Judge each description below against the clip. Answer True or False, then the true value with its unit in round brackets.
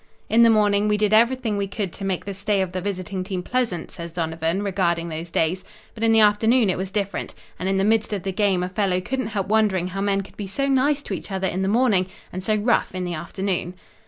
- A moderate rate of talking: False (250 wpm)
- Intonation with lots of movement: False (2.7 semitones)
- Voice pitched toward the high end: True (195 Hz)